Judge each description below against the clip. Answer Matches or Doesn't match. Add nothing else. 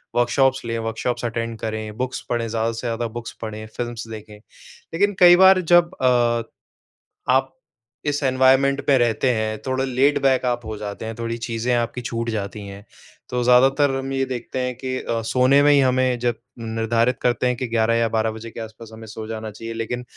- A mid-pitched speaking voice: Doesn't match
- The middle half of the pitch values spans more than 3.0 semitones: Doesn't match